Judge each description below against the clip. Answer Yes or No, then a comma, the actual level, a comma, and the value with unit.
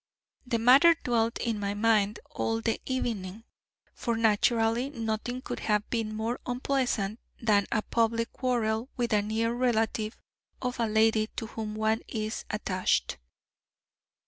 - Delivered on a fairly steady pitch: Yes, narrow, 1.9 semitones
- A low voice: No, high, 225 Hz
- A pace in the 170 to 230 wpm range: No, average, 140 wpm